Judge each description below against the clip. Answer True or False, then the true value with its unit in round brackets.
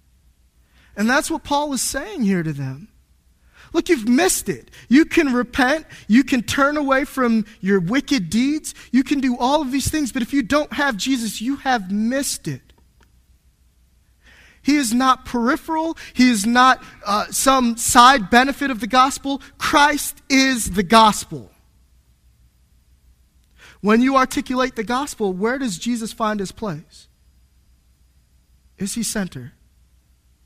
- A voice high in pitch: True (230 Hz)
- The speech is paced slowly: False (145 wpm)